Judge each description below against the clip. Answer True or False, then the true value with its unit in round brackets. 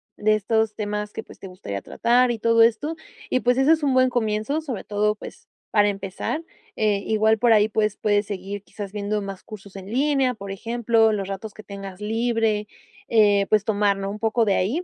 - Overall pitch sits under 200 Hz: False (215 Hz)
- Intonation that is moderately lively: False (2.3 semitones)